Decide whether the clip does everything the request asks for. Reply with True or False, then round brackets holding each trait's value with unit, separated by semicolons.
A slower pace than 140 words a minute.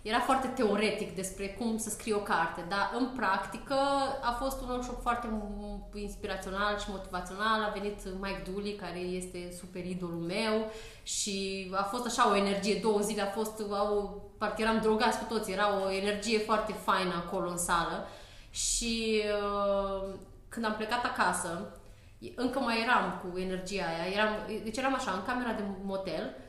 False (160 wpm)